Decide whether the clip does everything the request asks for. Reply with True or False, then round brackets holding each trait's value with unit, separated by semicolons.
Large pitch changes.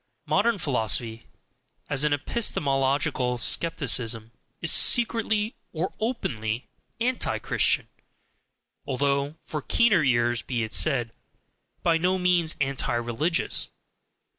True (6.8 semitones)